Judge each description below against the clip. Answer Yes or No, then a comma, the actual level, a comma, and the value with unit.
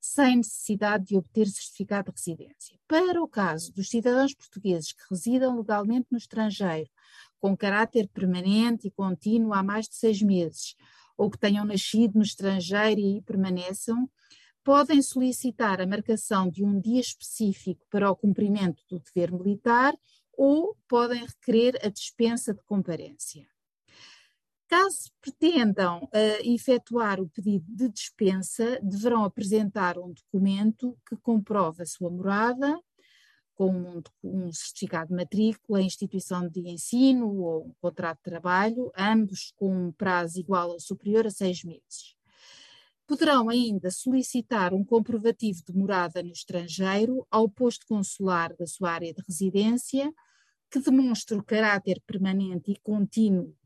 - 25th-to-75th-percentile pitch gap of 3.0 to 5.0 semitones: Yes, average, 4.0 semitones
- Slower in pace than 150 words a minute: Yes, average, 135 wpm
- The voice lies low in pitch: No, high, 205 Hz